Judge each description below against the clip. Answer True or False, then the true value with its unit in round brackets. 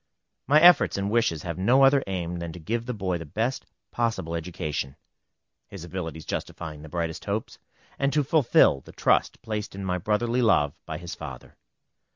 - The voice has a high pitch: False (95 Hz)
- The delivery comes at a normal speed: True (180 wpm)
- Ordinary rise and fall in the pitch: False (5.9 semitones)